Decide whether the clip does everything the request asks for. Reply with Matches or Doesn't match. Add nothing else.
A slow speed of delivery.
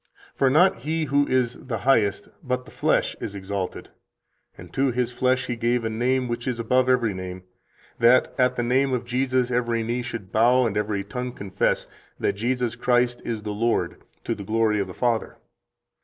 Doesn't match